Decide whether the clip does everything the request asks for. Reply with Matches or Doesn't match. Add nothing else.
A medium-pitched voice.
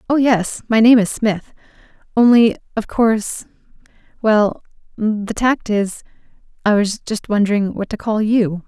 Doesn't match